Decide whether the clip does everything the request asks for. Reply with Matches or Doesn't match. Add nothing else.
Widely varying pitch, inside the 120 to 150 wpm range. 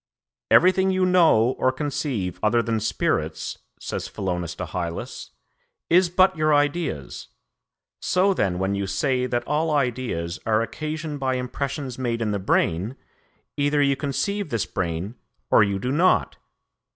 Matches